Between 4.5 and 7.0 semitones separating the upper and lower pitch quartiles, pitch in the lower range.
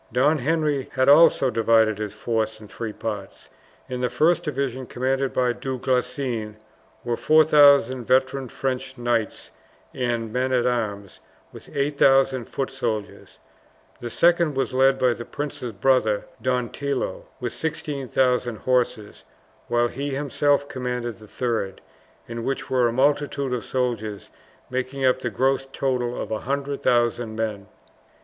No: narrow, 2.5 semitones; low, 125 Hz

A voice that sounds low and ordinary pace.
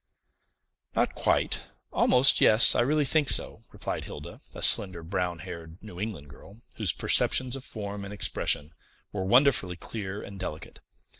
Yes: low, 100 Hz; average, 150 wpm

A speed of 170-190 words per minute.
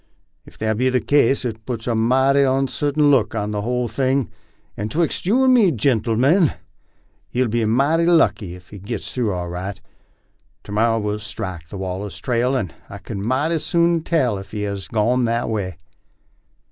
Yes: average, 180 wpm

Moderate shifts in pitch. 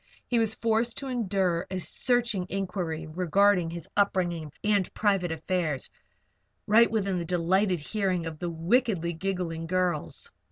Yes: average, 3.5 semitones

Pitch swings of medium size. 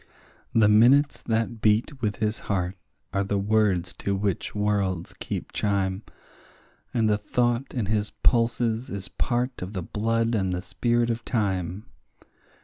Yes: average, 3.0 semitones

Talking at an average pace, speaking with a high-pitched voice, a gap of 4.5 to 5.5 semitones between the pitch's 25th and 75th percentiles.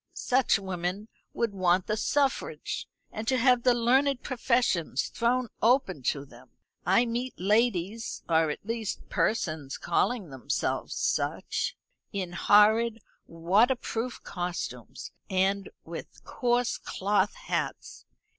No: slow, 115 wpm; high, 215 Hz; average, 5.2 semitones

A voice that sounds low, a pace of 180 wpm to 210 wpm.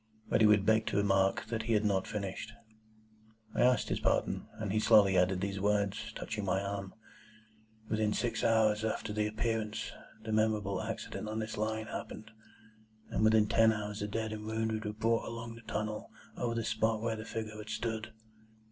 Yes: low, 110 Hz; average, 190 wpm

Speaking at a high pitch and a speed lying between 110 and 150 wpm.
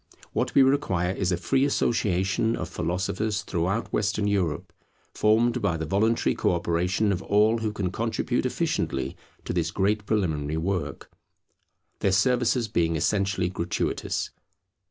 No: very low, 95 Hz; slow, 135 wpm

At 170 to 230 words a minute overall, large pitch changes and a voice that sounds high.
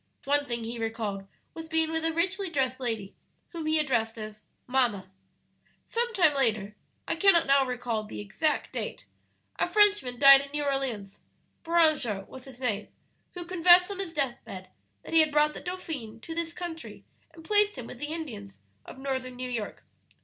Yes: average, 180 wpm; wide, 6.1 semitones; very high, 275 Hz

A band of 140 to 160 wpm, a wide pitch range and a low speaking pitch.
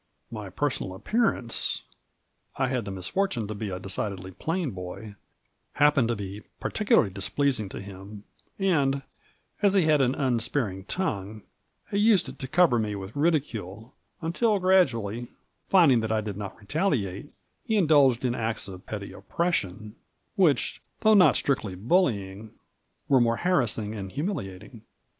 Yes: average, 150 wpm; wide, 7.5 semitones; low, 115 Hz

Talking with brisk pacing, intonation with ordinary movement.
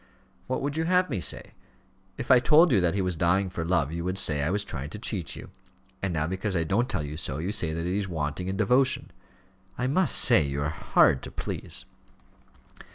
No: fast, 225 wpm; wide, 6.8 semitones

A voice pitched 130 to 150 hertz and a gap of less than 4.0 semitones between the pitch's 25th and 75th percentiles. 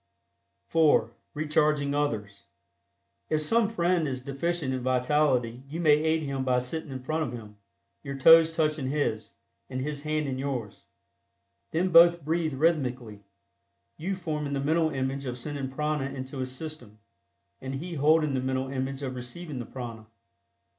Yes: medium, 140 Hz; average, 3.3 semitones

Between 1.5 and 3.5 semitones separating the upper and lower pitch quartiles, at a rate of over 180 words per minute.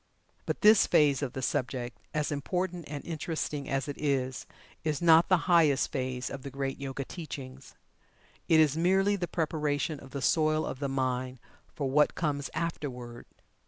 No: average, 3.1 semitones; average, 165 wpm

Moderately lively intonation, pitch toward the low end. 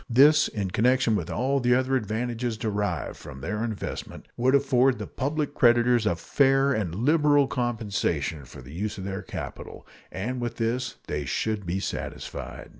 Yes: average, 4.7 semitones; low, 115 Hz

